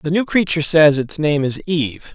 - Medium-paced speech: No, fast, 225 wpm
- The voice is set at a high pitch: No, medium, 155 Hz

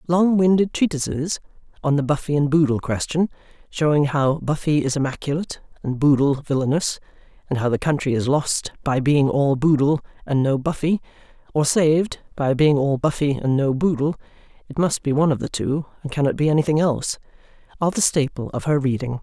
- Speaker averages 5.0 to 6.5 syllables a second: No, 4.7 syllables/s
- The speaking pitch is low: No, medium, 145 Hz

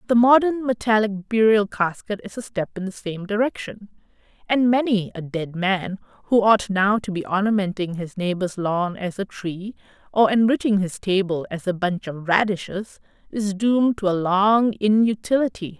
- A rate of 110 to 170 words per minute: Yes, average, 165 wpm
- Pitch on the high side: Yes, high, 205 Hz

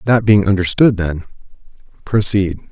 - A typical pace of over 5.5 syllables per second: No, 4.8 syllables/s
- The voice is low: Yes, low, 100 Hz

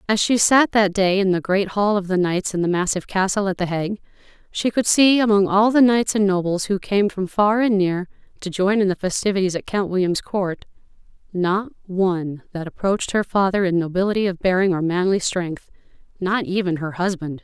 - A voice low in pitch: No, high, 190 Hz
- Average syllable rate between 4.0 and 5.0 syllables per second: No, 5.4 syllables/s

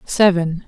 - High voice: No, medium, 180 Hz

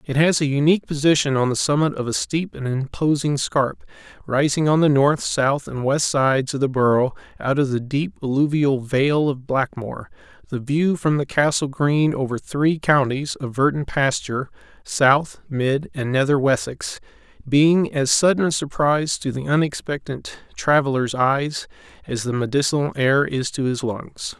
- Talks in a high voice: No, medium, 140 Hz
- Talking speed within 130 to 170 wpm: Yes, average, 160 wpm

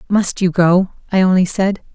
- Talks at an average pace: Yes, average, 185 wpm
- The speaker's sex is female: Yes, female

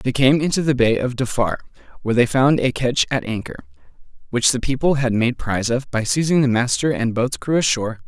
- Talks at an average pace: No, fast, 215 wpm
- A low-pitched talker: Yes, low, 130 Hz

